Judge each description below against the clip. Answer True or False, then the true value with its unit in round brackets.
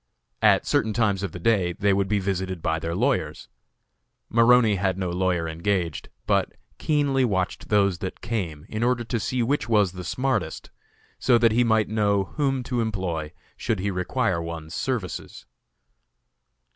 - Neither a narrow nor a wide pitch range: True (4.4 semitones)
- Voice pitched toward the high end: False (100 Hz)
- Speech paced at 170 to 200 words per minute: False (160 wpm)